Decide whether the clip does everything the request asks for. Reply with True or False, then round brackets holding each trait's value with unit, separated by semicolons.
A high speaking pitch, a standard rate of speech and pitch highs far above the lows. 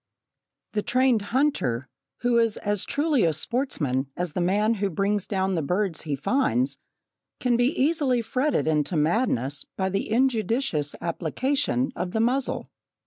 True (205 Hz; 145 wpm; 7.9 semitones)